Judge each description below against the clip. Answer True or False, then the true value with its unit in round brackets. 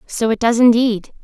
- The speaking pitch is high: True (230 Hz)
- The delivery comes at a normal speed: True (195 wpm)